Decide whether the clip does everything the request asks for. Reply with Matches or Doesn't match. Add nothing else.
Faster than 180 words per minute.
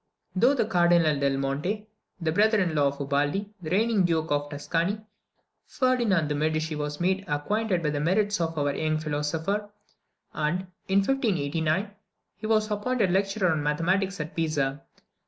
Doesn't match